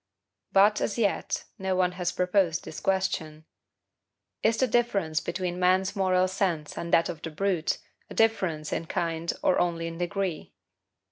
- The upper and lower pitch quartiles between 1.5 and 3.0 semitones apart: Yes, narrow, 2.6 semitones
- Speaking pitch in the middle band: Yes, medium, 180 Hz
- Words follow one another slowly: No, average, 155 wpm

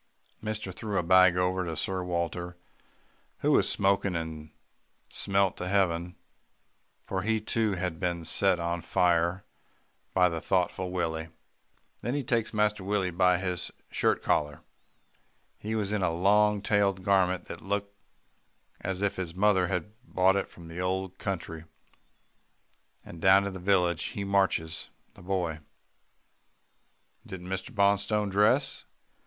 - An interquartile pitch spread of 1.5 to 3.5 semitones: Yes, narrow, 2.4 semitones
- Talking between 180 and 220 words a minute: No, average, 140 wpm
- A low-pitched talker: Yes, very low, 95 Hz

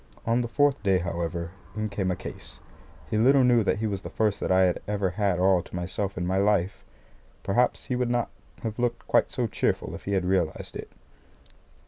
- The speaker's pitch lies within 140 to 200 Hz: No, low, 100 Hz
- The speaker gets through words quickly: Yes, fast, 210 wpm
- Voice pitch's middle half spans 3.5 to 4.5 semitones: Yes, average, 4.0 semitones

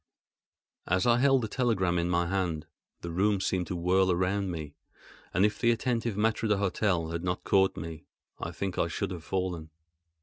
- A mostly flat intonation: No, average, 3.3 semitones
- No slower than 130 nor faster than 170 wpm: No, average, 180 wpm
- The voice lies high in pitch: No, very low, 95 Hz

